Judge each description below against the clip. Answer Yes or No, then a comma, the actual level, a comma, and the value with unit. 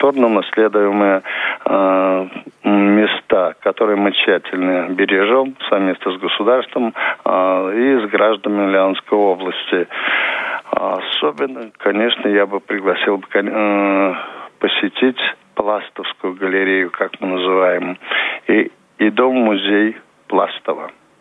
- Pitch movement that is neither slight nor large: No, narrow, 2.1 semitones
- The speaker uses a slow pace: Yes, slow, 90 wpm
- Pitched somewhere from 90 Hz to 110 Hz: Yes, low, 100 Hz